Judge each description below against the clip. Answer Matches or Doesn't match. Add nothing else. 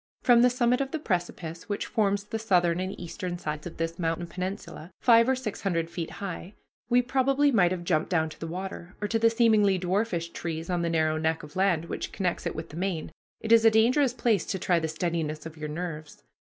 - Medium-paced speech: Doesn't match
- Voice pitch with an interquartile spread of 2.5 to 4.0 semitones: Doesn't match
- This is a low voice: Doesn't match